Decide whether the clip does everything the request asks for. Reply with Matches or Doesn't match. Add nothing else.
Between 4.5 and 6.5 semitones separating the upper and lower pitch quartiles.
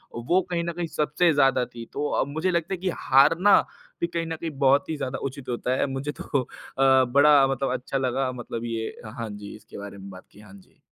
Matches